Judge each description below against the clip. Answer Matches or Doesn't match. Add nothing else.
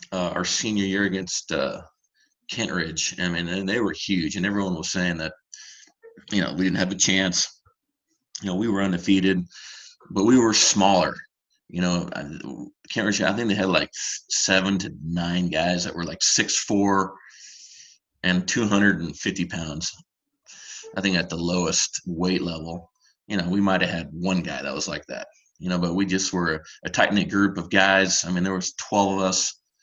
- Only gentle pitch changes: Matches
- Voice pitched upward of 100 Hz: Doesn't match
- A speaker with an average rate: Matches